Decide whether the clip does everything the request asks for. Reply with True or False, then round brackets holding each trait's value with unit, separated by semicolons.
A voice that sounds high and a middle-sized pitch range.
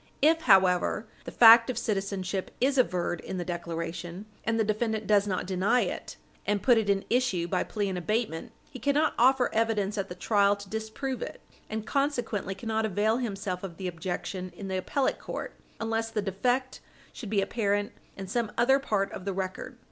True (205 Hz; 3.3 semitones)